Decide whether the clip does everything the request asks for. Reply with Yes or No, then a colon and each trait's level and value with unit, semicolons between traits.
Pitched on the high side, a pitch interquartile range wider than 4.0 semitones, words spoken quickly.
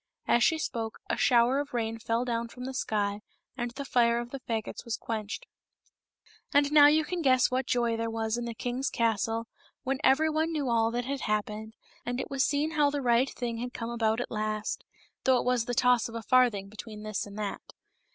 No: high, 240 Hz; average, 2.8 semitones; fast, 220 wpm